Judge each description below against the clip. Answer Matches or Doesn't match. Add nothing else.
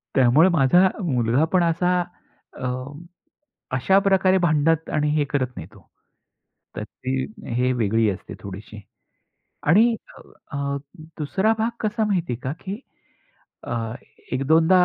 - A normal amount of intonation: Doesn't match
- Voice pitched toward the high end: Doesn't match